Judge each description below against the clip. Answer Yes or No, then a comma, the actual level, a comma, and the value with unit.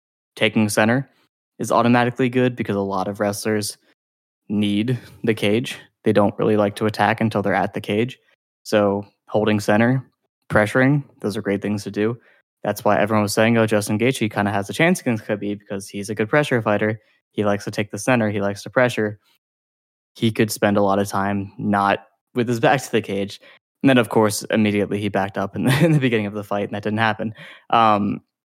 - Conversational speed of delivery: No, fast, 210 wpm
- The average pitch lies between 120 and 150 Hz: No, low, 105 Hz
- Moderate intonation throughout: No, narrow, 2.3 semitones